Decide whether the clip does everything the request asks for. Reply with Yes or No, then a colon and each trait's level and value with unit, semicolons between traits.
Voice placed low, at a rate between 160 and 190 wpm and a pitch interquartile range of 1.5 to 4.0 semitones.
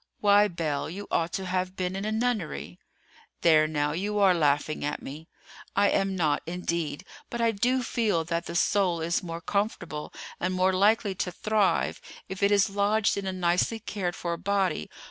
No: medium, 185 Hz; average, 185 wpm; average, 3.3 semitones